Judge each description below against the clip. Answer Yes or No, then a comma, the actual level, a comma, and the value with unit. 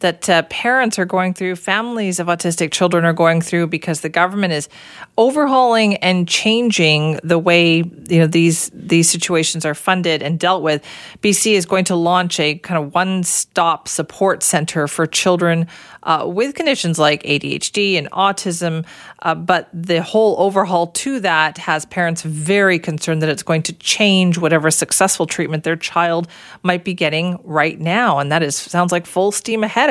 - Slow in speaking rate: No, average, 175 wpm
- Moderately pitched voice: Yes, medium, 175 Hz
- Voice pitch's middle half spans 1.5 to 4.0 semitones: Yes, narrow, 2.6 semitones